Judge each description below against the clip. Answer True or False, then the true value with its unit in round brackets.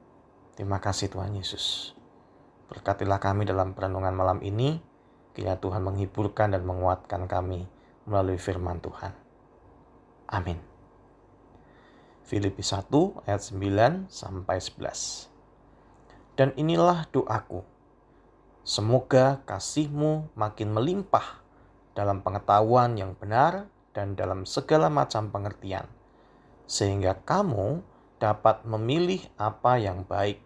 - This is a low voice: True (100 Hz)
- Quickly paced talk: False (95 wpm)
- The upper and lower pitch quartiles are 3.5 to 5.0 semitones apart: True (4.1 semitones)